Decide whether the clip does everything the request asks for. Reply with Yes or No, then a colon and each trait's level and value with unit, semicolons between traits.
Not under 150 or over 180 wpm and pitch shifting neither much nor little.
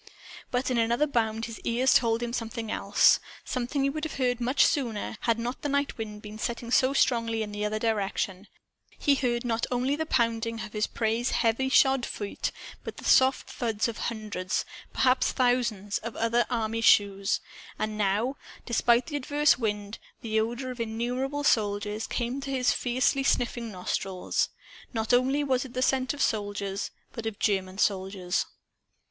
Yes: average, 170 wpm; average, 3.1 semitones